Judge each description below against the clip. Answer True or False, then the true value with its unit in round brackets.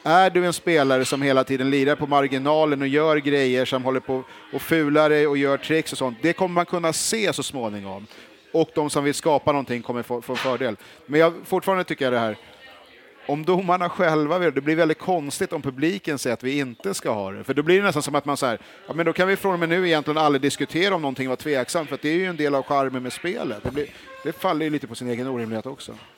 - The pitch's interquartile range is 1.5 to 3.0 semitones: False (3.7 semitones)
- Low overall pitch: False (145 Hz)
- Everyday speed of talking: False (260 wpm)